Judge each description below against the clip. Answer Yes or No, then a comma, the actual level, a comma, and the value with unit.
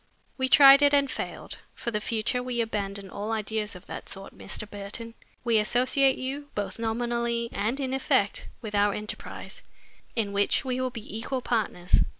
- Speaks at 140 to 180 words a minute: Yes, average, 170 wpm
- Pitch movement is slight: No, average, 3.7 semitones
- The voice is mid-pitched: No, high, 230 Hz